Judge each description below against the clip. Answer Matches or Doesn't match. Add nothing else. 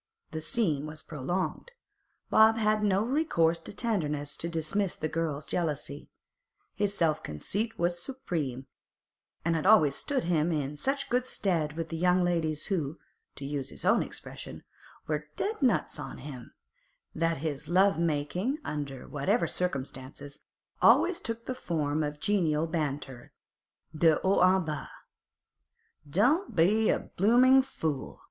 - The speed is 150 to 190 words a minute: Doesn't match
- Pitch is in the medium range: Matches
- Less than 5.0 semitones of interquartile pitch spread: Doesn't match